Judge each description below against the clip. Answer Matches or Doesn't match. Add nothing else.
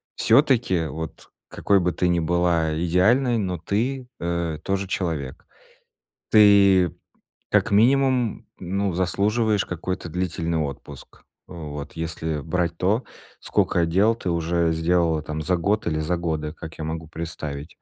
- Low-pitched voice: Matches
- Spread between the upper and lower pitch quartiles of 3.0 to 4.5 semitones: Matches